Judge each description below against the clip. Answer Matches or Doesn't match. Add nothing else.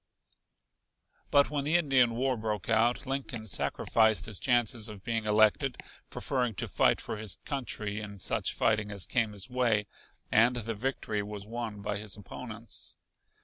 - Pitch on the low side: Matches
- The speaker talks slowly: Doesn't match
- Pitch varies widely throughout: Doesn't match